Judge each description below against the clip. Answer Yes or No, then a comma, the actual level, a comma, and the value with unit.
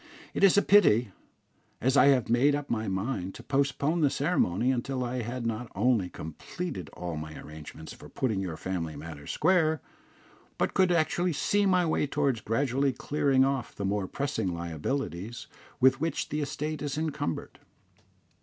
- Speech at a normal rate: Yes, average, 165 wpm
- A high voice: No, low, 130 Hz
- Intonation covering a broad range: Yes, wide, 7.3 semitones